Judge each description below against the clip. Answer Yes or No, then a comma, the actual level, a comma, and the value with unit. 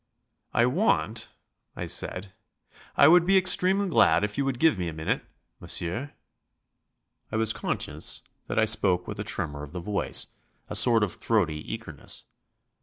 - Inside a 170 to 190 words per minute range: No, average, 160 wpm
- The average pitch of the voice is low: Yes, low, 110 Hz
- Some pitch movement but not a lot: No, wide, 7.7 semitones